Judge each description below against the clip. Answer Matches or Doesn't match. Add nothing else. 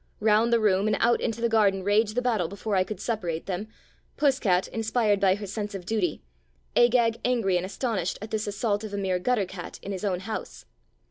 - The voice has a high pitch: Matches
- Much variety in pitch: Doesn't match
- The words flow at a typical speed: Doesn't match